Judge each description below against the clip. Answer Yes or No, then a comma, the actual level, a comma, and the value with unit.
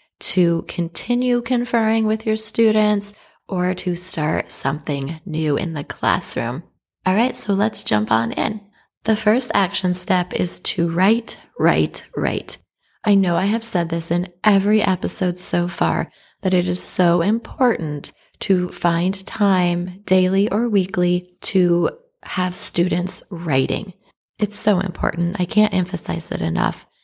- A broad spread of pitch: No, average, 3.5 semitones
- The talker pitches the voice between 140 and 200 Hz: Yes, medium, 185 Hz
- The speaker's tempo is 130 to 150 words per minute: Yes, average, 140 wpm